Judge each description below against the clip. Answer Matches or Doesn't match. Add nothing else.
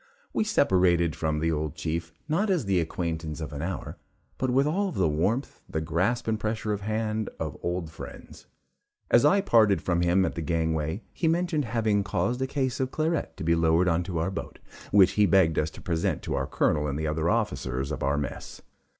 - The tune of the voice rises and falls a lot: Matches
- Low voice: Matches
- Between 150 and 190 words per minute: Doesn't match